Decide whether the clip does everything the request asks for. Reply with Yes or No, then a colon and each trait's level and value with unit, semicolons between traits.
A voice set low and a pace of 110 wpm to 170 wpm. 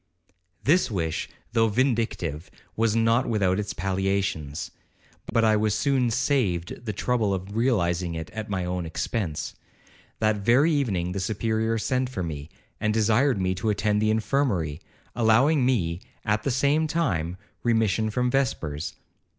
Yes: low, 110 Hz; average, 150 wpm